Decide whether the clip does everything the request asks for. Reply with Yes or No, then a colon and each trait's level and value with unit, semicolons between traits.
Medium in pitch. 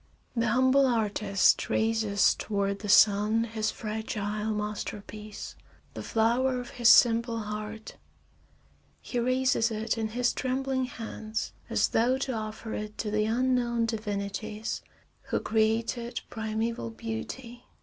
No: high, 220 Hz